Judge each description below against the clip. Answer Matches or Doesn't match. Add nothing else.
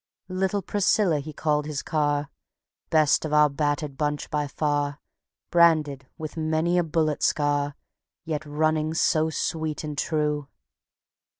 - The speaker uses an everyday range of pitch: Doesn't match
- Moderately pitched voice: Matches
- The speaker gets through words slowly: Matches